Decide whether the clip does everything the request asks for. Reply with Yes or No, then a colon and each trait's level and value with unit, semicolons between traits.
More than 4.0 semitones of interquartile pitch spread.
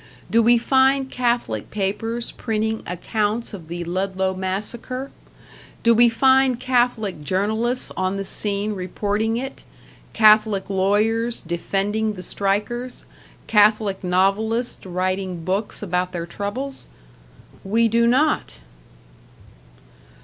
No: average, 3.6 semitones